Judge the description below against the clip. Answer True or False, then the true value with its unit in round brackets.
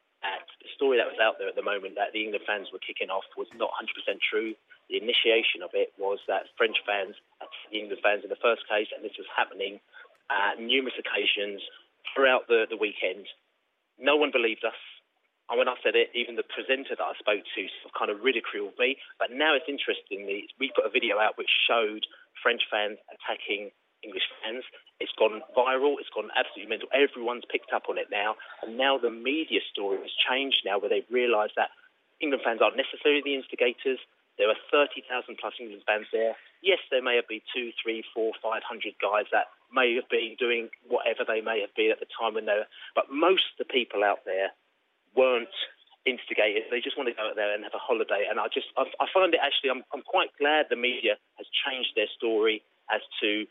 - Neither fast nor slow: False (215 wpm)